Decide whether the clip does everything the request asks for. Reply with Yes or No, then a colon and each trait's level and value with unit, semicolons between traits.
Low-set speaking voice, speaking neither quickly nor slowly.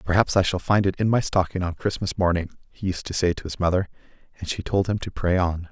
No: very low, 90 Hz; fast, 260 wpm